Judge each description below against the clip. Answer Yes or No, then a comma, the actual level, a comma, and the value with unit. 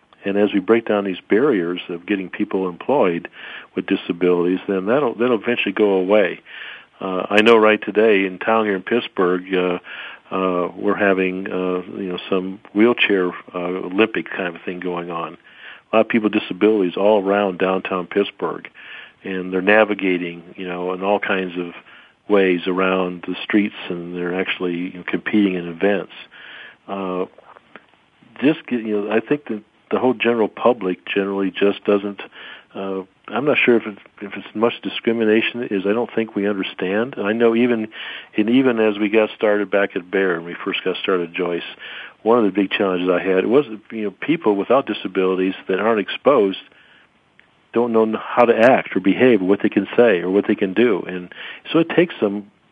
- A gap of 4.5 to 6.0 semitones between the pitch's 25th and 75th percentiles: No, average, 2.8 semitones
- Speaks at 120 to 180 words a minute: No, average, 190 wpm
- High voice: No, low, 100 Hz